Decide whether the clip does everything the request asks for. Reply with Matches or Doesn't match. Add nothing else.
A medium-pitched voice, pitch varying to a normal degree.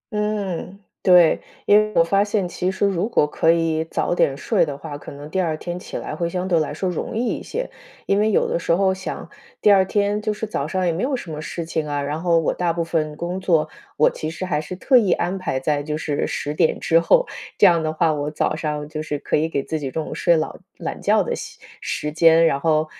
Matches